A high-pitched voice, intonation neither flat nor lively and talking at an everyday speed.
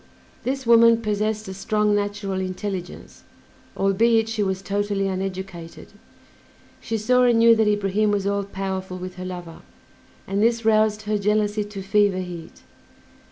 No: high, 205 Hz; narrow, 2.2 semitones; average, 145 wpm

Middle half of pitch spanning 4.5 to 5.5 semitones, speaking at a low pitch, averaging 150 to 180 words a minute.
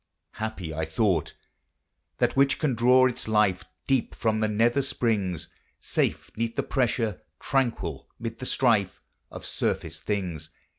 No: average, 4.9 semitones; low, 110 Hz; average, 140 wpm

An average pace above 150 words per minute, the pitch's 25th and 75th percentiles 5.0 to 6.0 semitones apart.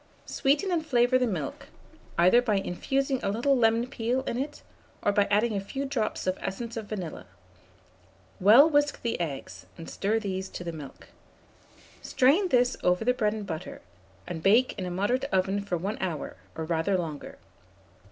Yes: average, 175 wpm; wide, 5.5 semitones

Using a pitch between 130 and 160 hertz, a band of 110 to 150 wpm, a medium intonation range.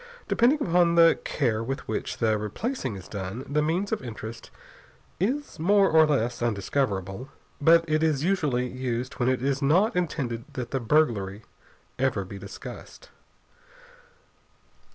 No: low, 135 Hz; average, 140 wpm; wide, 6.4 semitones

